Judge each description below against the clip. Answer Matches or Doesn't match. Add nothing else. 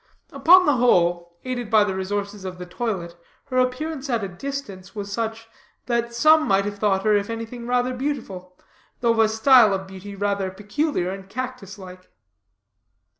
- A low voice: Doesn't match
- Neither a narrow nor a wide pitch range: Matches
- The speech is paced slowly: Doesn't match